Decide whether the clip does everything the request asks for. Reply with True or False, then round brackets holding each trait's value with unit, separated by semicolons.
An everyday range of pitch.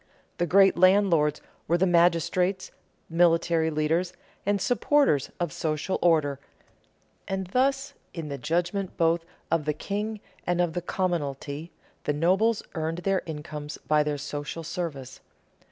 True (3.5 semitones)